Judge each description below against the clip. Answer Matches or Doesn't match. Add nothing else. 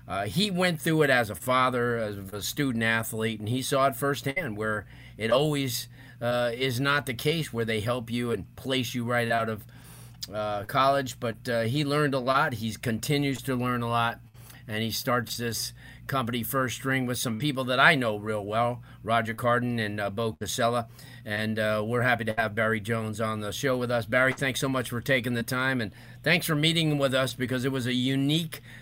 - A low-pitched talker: Matches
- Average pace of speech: Doesn't match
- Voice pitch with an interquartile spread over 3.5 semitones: Doesn't match